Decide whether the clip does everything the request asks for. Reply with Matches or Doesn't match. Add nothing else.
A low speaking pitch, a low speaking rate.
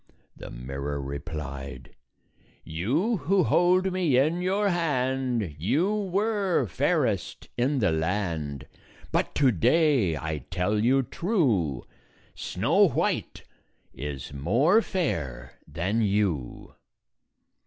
Matches